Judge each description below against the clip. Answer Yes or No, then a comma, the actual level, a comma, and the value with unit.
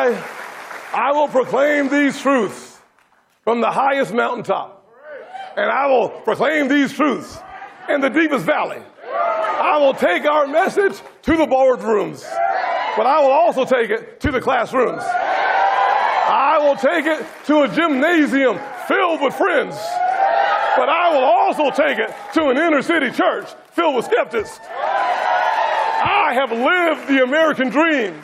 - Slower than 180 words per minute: Yes, average, 140 wpm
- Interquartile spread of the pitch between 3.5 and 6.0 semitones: Yes, average, 4.1 semitones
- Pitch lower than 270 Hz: No, very high, 300 Hz